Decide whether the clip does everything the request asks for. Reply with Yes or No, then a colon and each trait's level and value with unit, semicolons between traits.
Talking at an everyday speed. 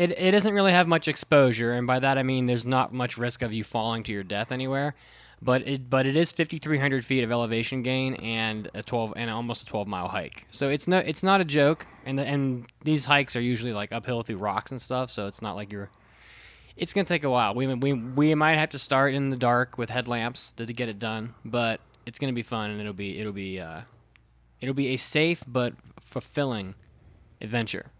No: fast, 230 wpm